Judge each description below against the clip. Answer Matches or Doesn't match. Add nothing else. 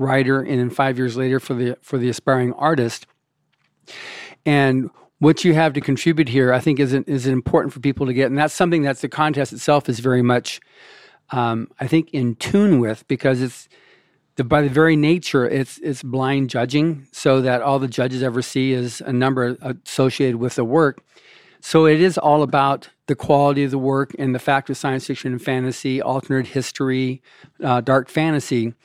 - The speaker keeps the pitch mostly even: Matches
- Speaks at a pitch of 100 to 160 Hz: Matches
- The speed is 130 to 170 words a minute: Doesn't match